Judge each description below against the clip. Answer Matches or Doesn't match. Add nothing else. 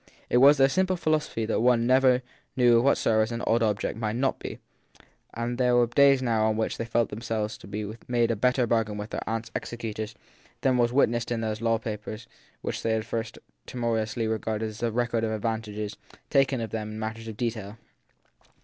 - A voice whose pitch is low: Matches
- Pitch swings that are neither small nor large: Doesn't match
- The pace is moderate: Doesn't match